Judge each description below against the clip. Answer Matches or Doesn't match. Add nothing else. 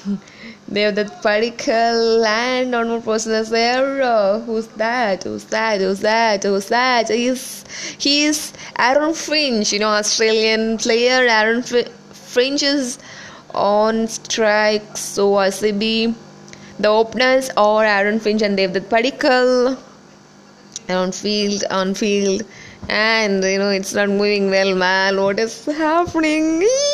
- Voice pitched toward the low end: Doesn't match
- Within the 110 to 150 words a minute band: Matches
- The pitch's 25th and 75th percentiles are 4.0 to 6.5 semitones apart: Doesn't match